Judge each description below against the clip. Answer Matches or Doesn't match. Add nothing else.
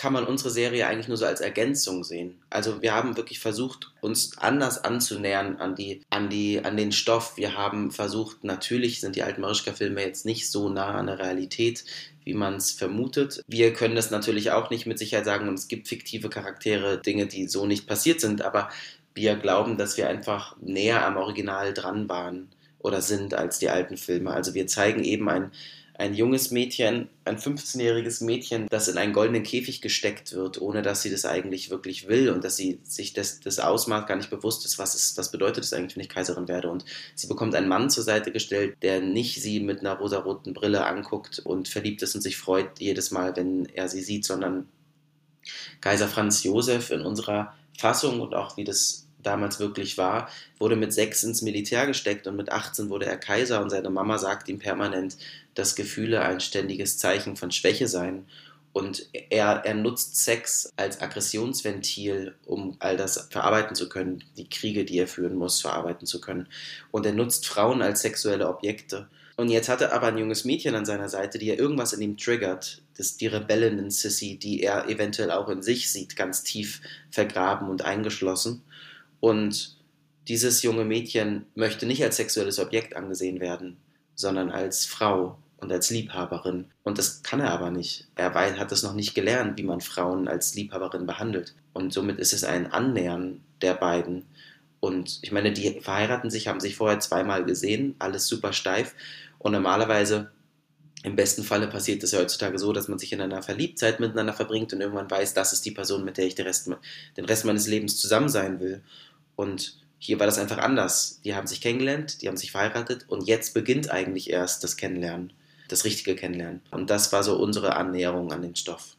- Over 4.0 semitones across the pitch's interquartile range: Doesn't match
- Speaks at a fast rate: Matches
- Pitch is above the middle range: Doesn't match